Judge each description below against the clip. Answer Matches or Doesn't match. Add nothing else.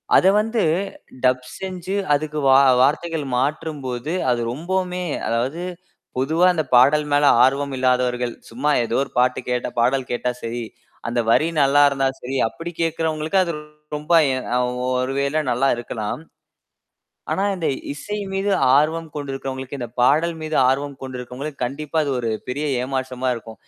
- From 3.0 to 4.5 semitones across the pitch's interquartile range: Matches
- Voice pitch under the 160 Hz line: Matches